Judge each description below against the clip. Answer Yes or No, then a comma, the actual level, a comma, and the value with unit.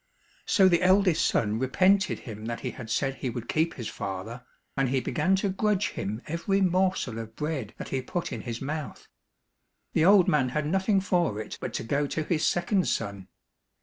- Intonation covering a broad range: Yes, wide, 7.9 semitones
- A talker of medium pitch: Yes, medium, 150 Hz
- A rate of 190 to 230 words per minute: Yes, average, 195 wpm